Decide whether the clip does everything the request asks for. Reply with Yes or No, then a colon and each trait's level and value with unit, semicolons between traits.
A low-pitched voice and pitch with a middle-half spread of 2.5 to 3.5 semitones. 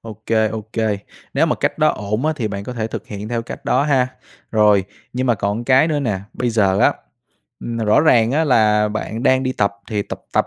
Yes: low, 110 Hz; average, 3.1 semitones